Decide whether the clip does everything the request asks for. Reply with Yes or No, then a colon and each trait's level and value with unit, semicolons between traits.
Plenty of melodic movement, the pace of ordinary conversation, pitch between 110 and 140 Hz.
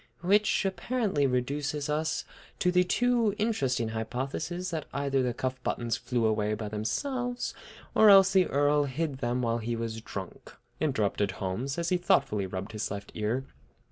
Yes: wide, 8.0 semitones; average, 160 wpm; low, 135 Hz